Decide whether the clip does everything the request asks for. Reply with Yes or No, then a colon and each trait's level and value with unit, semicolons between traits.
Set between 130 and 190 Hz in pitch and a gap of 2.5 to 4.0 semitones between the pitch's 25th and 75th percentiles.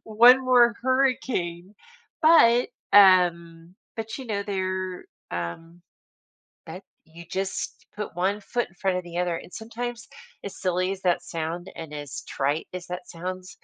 No: medium, 185 Hz; average, 4.4 semitones